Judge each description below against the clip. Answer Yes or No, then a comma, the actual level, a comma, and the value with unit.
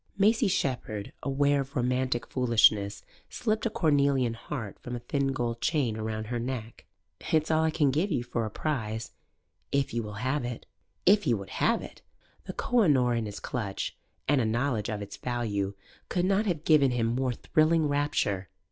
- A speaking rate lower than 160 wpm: No, average, 185 wpm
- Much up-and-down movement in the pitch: No, average, 4.8 semitones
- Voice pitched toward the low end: Yes, low, 125 Hz